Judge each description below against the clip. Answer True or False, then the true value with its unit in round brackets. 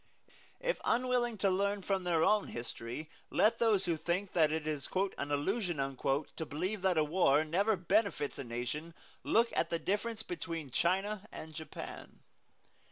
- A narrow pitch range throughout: False (4.9 semitones)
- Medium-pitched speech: True (175 Hz)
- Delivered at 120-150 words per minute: False (160 wpm)